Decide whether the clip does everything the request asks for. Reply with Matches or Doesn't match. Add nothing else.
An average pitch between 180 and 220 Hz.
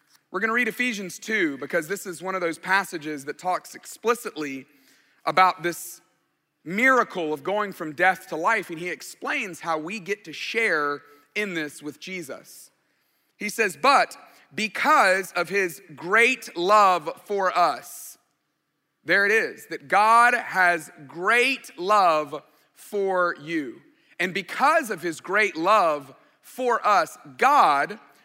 Matches